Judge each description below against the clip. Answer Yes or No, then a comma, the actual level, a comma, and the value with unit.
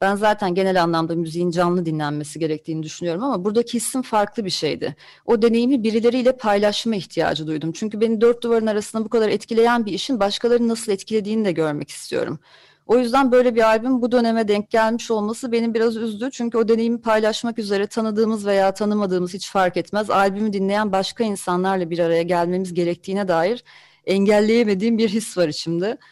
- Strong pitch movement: No, average, 3.8 semitones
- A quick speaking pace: Yes, fast, 170 wpm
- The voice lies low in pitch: No, high, 215 Hz